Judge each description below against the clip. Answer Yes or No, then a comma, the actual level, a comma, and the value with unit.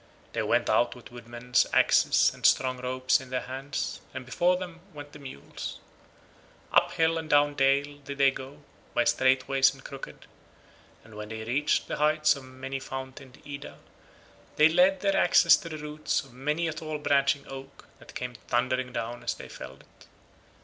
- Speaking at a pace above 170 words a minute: Yes, average, 180 wpm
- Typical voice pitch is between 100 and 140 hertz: Yes, low, 135 Hz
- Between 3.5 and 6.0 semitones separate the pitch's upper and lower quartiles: No, average, 2.7 semitones